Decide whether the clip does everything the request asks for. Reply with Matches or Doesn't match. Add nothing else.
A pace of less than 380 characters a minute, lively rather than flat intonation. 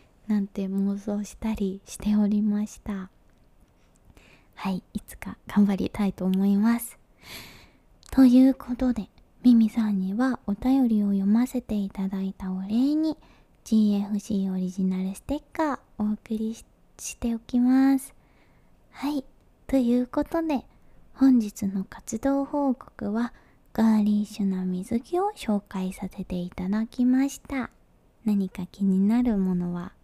Doesn't match